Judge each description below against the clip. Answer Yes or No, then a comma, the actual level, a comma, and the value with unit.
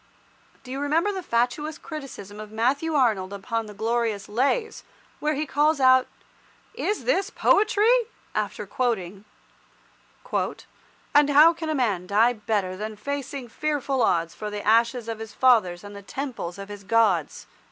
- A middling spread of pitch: No, wide, 5.8 semitones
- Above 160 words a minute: No, average, 150 wpm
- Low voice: No, high, 235 Hz